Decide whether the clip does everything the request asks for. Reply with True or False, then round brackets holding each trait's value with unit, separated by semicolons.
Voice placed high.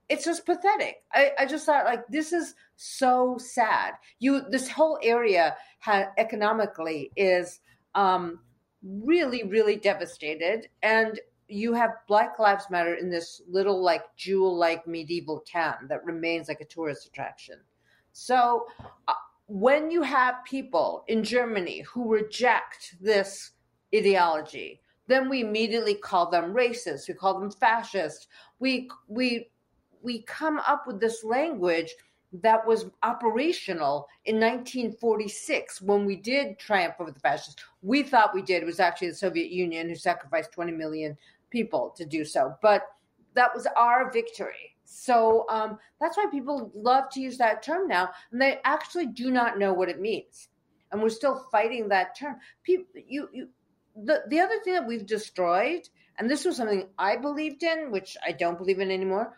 True (225 Hz)